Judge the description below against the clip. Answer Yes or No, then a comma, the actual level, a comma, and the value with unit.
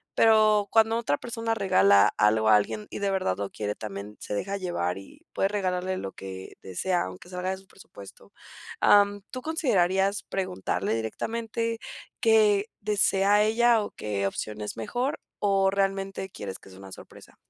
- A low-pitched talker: No, high, 190 Hz